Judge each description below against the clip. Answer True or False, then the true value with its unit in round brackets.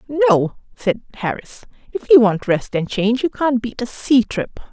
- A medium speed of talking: True (190 wpm)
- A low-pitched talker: False (235 Hz)